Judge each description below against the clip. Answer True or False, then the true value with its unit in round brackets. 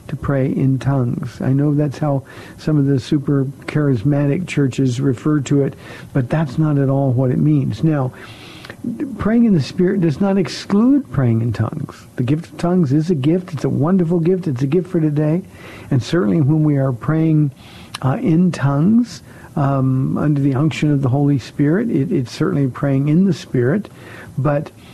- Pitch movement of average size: True (3.3 semitones)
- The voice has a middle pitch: True (150 Hz)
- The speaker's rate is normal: True (180 wpm)